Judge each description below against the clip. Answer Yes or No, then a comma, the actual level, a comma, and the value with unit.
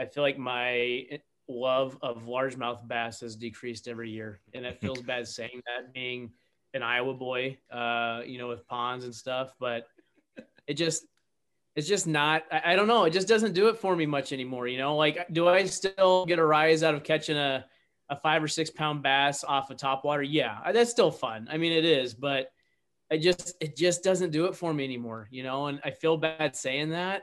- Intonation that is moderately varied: Yes, average, 4.5 semitones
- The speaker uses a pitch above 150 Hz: No, medium, 140 Hz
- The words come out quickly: Yes, fast, 210 wpm